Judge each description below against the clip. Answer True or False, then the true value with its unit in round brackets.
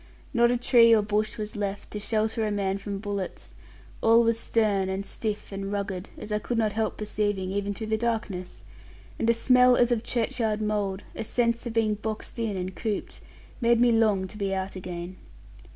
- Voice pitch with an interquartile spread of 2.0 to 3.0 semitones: True (2.5 semitones)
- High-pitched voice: True (215 Hz)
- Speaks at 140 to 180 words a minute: False (200 wpm)